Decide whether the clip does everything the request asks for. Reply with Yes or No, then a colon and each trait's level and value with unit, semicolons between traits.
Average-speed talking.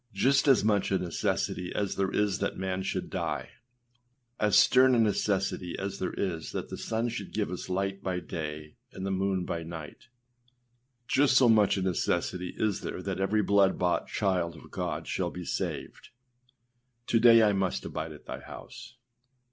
Yes: average, 180 wpm